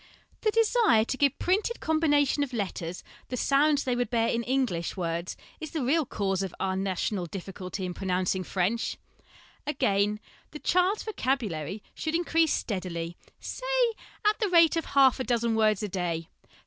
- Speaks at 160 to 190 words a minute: Yes, average, 165 wpm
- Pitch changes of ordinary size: No, wide, 8.6 semitones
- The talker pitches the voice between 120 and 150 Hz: No, high, 235 Hz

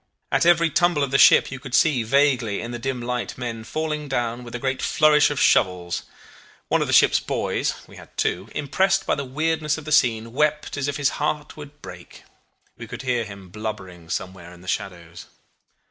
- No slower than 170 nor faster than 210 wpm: Yes, fast, 205 wpm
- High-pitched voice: No, low, 130 Hz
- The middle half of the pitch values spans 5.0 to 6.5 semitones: Yes, wide, 5.4 semitones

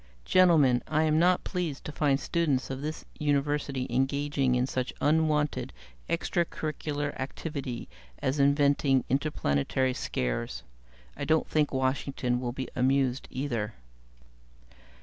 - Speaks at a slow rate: Yes, slow, 120 wpm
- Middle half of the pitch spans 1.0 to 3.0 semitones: Yes, narrow, 2.6 semitones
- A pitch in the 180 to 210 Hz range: No, medium, 140 Hz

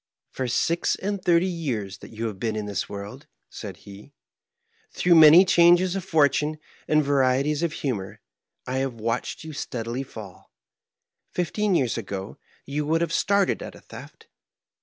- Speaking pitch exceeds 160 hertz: No, medium, 140 Hz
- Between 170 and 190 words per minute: No, average, 160 wpm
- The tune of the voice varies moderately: No, wide, 7.0 semitones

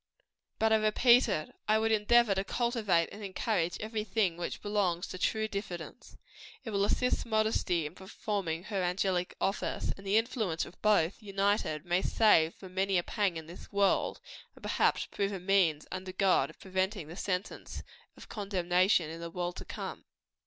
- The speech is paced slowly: No, average, 175 wpm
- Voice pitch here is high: Yes, high, 195 Hz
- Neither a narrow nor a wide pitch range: Yes, average, 3.2 semitones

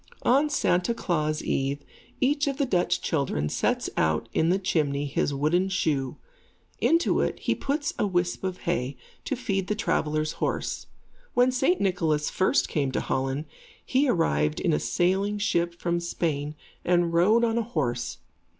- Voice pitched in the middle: Yes, medium, 175 Hz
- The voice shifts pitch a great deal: Yes, wide, 6.5 semitones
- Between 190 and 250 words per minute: No, average, 160 wpm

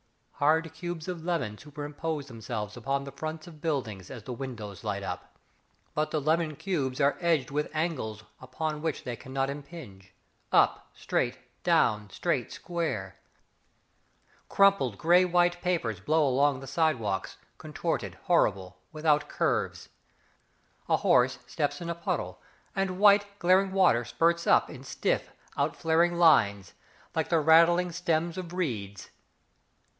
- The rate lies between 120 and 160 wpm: Yes, average, 140 wpm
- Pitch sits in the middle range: Yes, medium, 150 Hz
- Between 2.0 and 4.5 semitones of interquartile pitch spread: No, average, 5.2 semitones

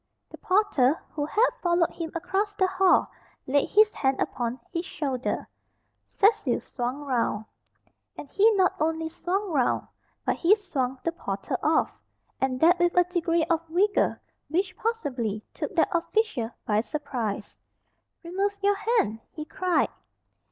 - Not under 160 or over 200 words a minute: No, average, 145 wpm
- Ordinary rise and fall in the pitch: No, wide, 6.1 semitones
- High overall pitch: Yes, very high, 335 Hz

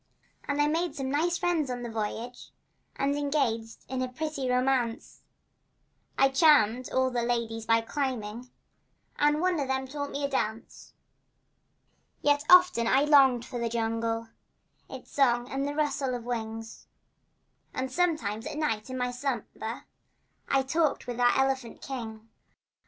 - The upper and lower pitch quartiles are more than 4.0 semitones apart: No, average, 3.7 semitones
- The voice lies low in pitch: No, very high, 260 Hz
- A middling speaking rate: Yes, average, 150 wpm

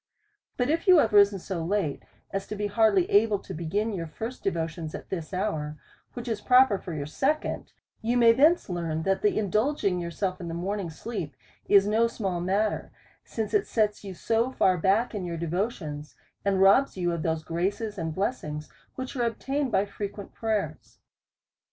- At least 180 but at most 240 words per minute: Yes, average, 190 wpm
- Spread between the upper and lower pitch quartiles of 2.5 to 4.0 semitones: No, average, 4.6 semitones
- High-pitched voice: Yes, high, 200 Hz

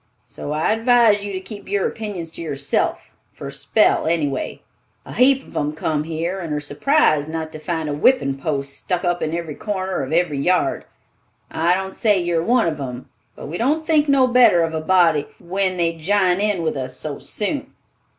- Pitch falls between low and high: Yes, medium, 175 Hz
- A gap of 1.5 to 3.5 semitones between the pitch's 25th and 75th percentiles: No, average, 4.8 semitones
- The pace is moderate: No, fast, 210 wpm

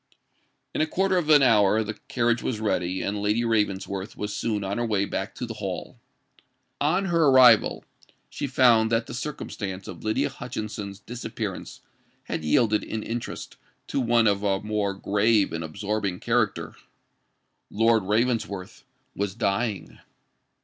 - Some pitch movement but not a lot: Yes, average, 3.0 semitones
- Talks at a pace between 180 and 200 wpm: No, average, 150 wpm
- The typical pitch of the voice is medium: No, low, 110 Hz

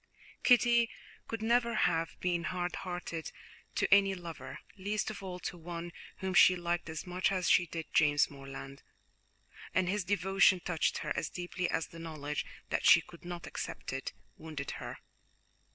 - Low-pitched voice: No, medium, 175 Hz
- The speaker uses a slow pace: No, average, 165 wpm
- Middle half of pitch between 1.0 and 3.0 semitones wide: Yes, average, 2.7 semitones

